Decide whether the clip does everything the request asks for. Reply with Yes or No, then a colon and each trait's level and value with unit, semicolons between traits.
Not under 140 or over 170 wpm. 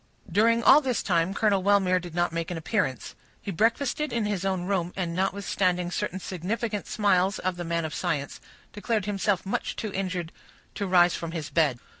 No: average, 185 wpm